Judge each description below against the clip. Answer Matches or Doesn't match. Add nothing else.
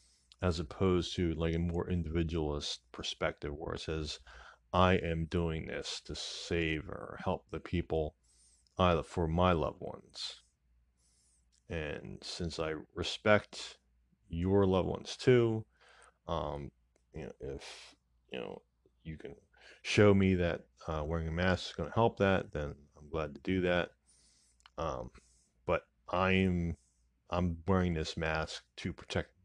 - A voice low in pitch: Matches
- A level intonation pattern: Doesn't match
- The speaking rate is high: Doesn't match